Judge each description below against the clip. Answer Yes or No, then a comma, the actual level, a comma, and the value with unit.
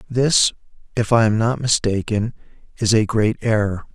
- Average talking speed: Yes, average, 150 wpm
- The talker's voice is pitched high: No, low, 110 Hz